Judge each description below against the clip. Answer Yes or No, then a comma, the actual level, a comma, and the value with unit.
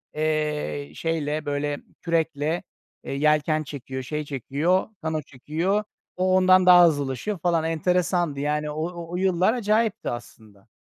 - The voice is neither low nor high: Yes, medium, 155 Hz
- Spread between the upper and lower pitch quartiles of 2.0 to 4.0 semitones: Yes, average, 3.6 semitones